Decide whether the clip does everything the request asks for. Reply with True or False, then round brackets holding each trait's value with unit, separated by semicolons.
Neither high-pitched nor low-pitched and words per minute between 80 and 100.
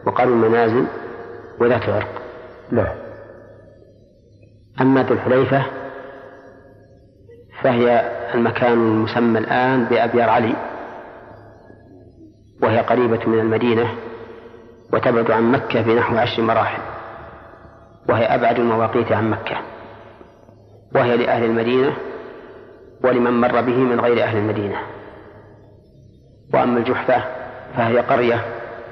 False (115 Hz; 85 wpm)